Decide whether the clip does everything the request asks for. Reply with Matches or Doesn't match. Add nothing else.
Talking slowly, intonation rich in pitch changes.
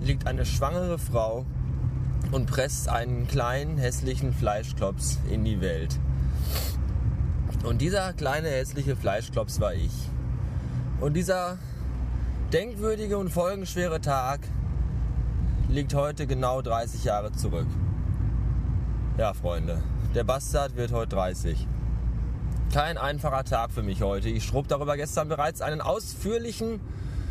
Matches